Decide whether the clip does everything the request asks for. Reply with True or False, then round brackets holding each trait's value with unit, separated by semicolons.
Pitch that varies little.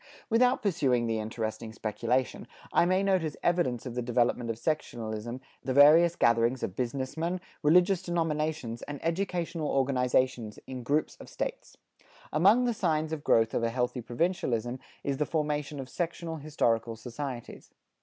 False (5.6 semitones)